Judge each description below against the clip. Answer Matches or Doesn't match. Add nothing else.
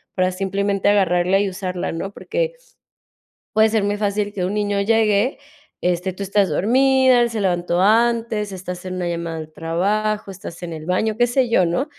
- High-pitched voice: Matches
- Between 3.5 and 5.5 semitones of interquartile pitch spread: Doesn't match